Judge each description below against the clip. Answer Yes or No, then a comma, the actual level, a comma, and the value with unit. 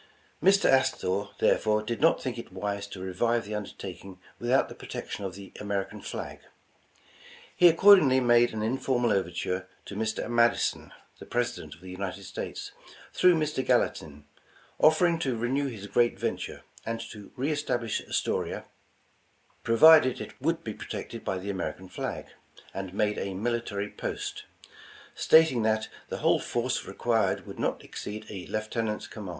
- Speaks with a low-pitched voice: Yes, low, 110 Hz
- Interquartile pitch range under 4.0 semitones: No, average, 4.7 semitones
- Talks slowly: No, average, 155 wpm